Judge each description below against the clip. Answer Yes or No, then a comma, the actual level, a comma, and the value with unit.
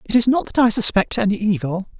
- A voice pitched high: Yes, high, 220 Hz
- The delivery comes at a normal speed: No, fast, 240 wpm